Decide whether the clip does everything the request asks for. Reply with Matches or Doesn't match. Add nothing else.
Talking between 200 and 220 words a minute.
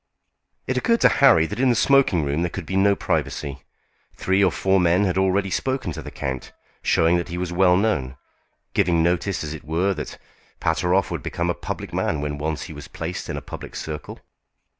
Matches